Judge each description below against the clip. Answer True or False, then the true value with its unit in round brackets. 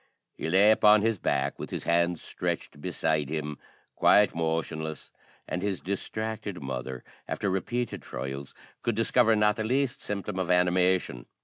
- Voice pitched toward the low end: True (90 Hz)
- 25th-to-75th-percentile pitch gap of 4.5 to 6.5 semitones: True (5.1 semitones)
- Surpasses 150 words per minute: False (145 wpm)